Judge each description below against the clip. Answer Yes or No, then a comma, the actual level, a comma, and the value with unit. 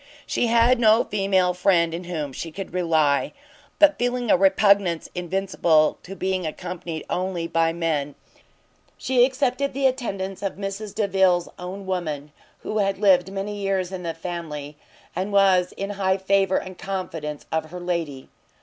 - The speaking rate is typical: Yes, average, 160 wpm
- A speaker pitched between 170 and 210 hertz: Yes, medium, 185 Hz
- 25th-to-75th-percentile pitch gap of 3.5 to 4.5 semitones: No, average, 2.8 semitones